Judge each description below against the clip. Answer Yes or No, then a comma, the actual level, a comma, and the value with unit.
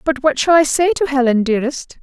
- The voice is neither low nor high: No, very high, 280 Hz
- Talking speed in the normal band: No, fast, 235 wpm